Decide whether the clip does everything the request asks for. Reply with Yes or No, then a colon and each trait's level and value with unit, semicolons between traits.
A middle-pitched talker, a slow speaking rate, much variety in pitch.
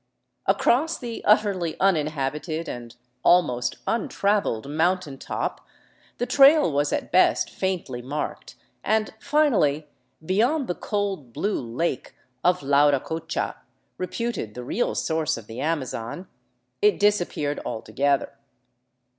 Yes: medium, 165 Hz; slow, 115 wpm; wide, 6.7 semitones